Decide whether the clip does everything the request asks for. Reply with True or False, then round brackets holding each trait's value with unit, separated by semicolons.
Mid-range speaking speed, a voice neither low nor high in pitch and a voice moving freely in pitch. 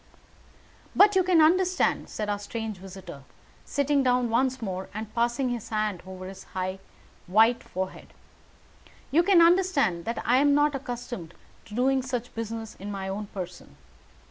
False (155 wpm; 230 Hz; 5.9 semitones)